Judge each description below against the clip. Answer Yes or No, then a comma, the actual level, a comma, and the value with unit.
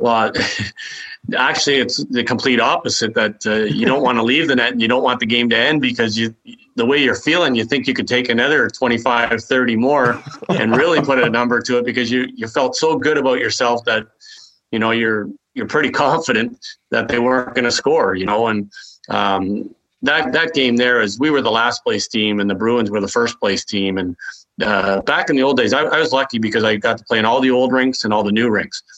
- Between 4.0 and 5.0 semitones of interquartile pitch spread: No, average, 2.8 semitones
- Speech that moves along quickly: Yes, fast, 240 wpm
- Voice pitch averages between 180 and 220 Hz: No, low, 120 Hz